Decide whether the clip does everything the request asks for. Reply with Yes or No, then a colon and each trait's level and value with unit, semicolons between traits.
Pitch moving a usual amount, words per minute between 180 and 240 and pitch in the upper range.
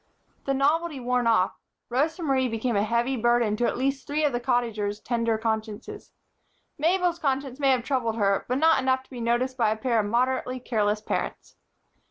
Yes: average, 3.1 semitones; average, 190 wpm; high, 245 Hz